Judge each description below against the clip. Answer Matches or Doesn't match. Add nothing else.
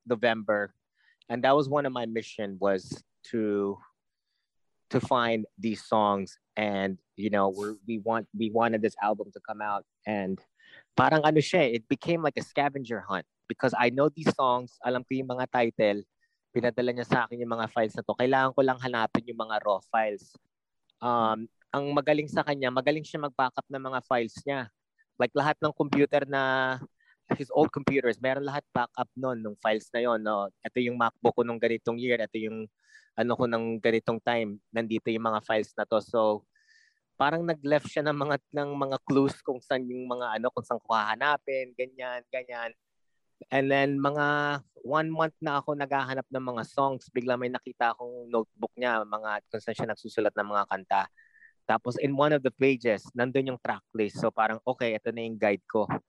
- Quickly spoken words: Matches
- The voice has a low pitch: Matches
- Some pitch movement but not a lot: Matches